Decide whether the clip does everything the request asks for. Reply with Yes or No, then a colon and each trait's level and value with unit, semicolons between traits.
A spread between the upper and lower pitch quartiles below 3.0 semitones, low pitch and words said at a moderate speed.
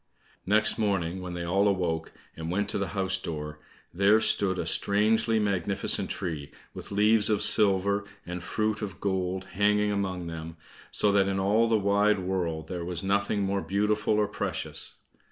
Yes: narrow, 2.5 semitones; low, 100 Hz; average, 170 wpm